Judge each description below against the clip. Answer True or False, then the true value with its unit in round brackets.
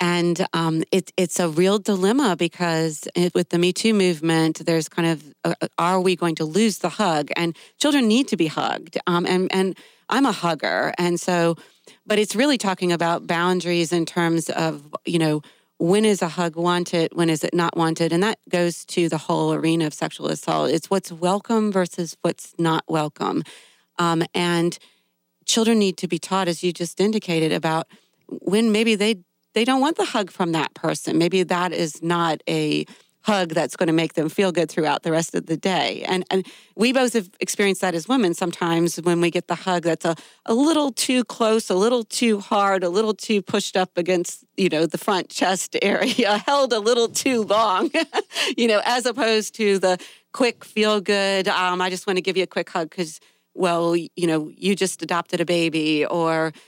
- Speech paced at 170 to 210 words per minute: True (200 wpm)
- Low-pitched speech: False (180 Hz)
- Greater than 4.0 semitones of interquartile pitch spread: False (3.7 semitones)